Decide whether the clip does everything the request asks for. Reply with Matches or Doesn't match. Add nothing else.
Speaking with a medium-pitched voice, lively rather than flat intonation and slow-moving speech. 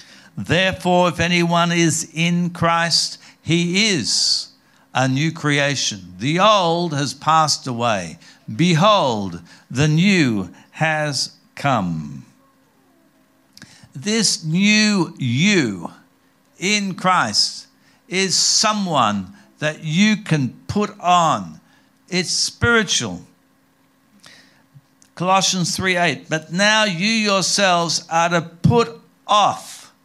Doesn't match